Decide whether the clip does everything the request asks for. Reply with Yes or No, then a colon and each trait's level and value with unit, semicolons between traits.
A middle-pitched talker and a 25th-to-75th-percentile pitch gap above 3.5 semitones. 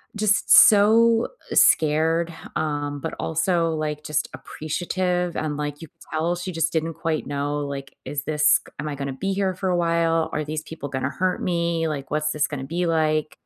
No: medium, 160 Hz; average, 2.7 semitones